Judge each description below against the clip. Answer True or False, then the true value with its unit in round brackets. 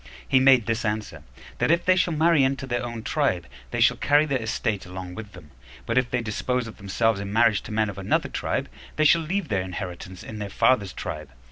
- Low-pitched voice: True (115 Hz)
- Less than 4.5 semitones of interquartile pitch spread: False (5.2 semitones)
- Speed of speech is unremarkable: False (225 wpm)